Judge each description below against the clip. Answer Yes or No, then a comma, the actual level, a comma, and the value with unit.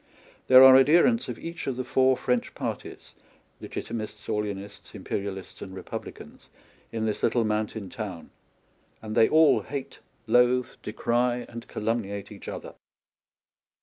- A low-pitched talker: Yes, low, 115 Hz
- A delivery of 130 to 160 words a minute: Yes, average, 140 wpm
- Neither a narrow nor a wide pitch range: Yes, average, 3.3 semitones